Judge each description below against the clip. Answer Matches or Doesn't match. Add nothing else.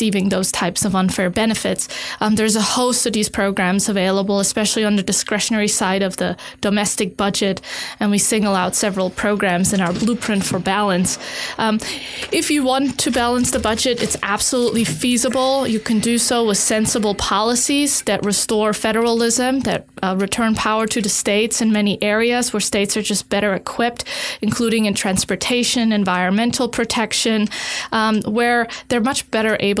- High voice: Matches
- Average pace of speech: Matches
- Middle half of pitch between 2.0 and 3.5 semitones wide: Matches